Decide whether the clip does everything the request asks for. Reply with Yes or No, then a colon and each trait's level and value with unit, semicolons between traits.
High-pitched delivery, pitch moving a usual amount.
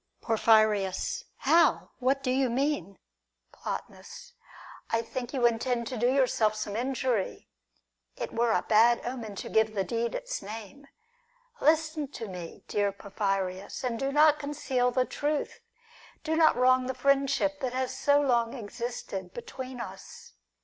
Yes: high, 245 Hz; average, 4.1 semitones